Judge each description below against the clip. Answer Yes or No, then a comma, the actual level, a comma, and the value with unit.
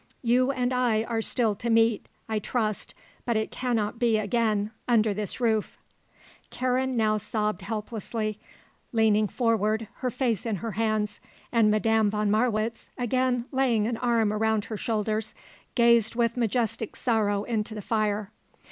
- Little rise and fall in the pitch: Yes, narrow, 1.8 semitones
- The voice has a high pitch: Yes, high, 225 Hz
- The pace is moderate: Yes, average, 145 wpm